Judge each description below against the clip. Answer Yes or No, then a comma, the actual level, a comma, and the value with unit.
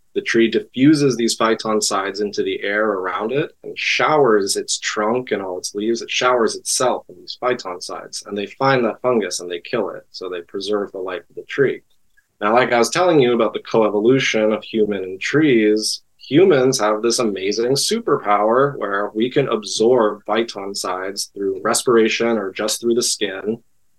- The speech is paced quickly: No, average, 190 wpm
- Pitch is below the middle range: Yes, low, 115 Hz